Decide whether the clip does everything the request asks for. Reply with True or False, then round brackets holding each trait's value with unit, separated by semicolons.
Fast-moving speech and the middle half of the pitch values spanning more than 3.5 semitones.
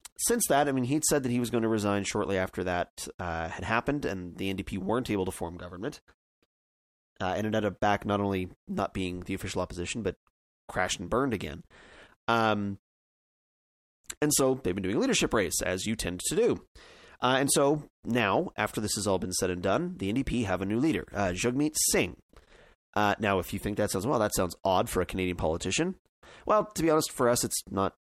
True (215 wpm; 4.7 semitones)